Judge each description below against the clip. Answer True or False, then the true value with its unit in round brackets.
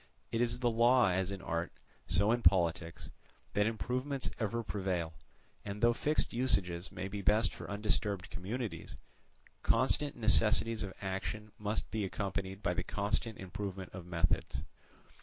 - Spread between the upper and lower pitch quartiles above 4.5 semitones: False (3.5 semitones)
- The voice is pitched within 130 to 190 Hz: False (100 Hz)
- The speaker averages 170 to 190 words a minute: False (145 wpm)